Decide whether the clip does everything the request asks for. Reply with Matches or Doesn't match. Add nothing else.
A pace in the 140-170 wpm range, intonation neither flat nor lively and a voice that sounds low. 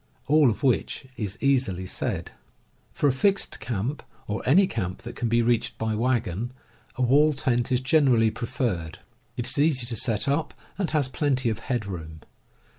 Doesn't match